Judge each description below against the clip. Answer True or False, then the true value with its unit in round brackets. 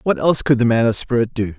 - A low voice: True (120 Hz)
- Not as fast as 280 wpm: False (300 wpm)